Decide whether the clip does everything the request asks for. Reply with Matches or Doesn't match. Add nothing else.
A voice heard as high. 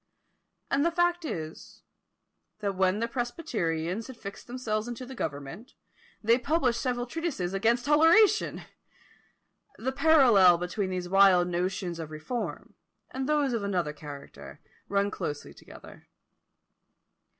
Matches